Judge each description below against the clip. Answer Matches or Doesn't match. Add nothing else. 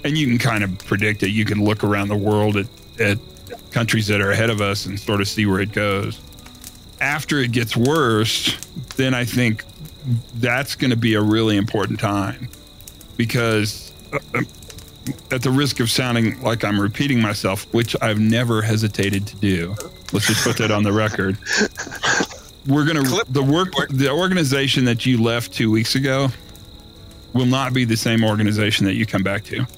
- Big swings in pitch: Doesn't match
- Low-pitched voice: Matches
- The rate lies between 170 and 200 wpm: Matches